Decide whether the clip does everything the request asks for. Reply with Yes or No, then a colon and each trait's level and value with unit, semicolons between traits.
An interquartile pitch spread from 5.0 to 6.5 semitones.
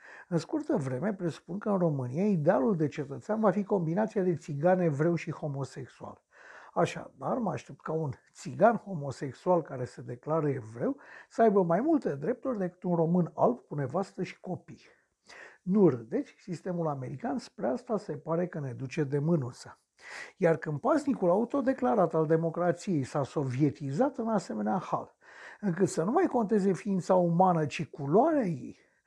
Yes: wide, 5.5 semitones